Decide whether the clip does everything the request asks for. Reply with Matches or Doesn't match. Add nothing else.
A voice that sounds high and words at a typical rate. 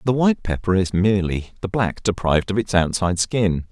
Doesn't match